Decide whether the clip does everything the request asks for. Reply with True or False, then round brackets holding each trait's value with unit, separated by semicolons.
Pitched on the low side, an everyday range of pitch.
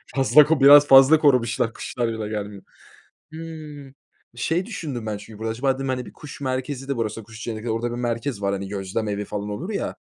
True (120 Hz; 4.5 semitones)